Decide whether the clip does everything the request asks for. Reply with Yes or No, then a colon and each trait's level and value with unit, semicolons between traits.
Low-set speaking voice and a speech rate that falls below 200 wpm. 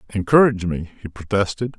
Yes: low, 100 Hz; slow, 135 wpm